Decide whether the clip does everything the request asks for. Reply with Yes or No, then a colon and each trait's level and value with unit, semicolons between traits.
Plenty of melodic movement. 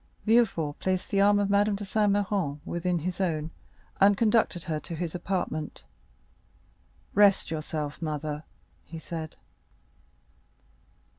No: average, 4.3 semitones